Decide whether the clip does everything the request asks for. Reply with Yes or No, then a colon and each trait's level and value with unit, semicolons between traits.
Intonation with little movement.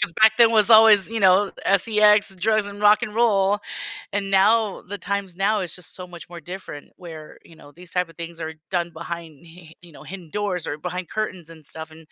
No: average, 3.6 semitones